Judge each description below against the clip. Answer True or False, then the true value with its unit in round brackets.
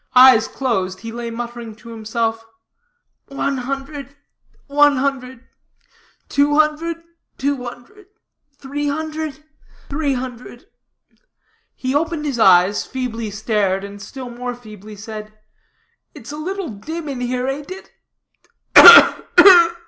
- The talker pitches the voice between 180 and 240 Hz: False (255 Hz)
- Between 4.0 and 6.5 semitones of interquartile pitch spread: True (4.3 semitones)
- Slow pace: True (110 wpm)